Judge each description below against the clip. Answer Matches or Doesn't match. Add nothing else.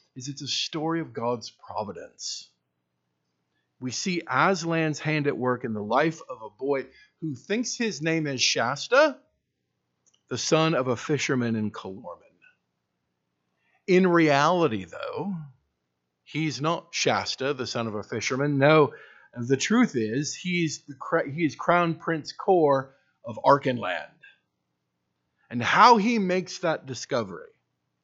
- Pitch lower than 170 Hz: Matches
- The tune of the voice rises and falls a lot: Matches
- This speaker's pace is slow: Matches